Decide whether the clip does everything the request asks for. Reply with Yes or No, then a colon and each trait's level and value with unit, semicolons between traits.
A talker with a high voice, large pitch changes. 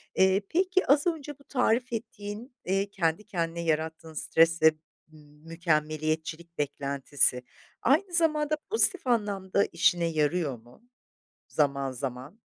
No: medium, 170 Hz; wide, 7.5 semitones